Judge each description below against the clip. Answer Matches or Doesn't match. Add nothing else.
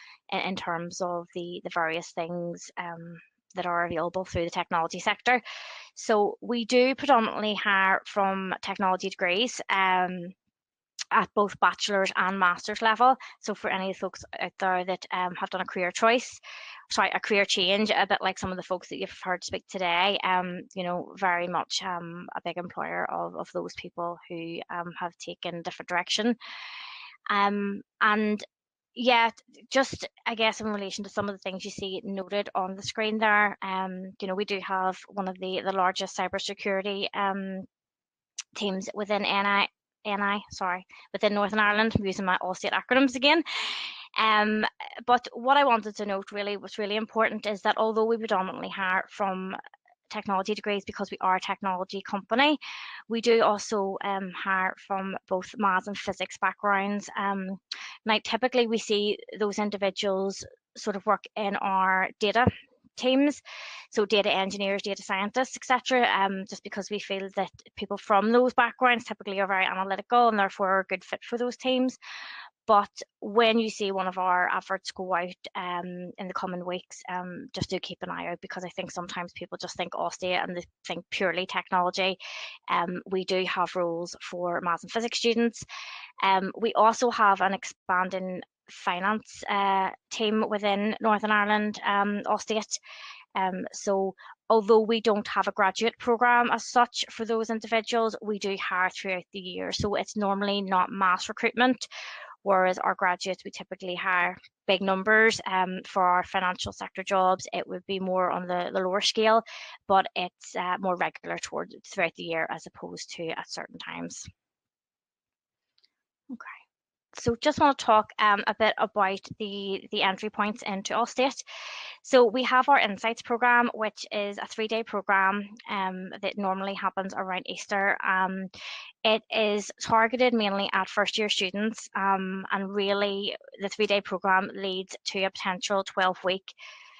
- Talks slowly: Doesn't match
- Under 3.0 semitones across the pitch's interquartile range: Matches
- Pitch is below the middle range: Doesn't match